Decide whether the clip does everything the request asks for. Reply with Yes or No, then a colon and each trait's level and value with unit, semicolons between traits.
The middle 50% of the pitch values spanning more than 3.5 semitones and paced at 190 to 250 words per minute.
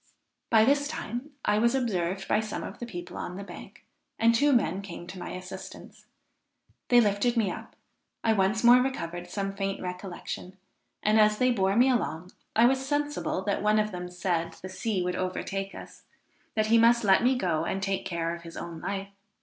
Yes: average, 4.3 semitones; average, 200 wpm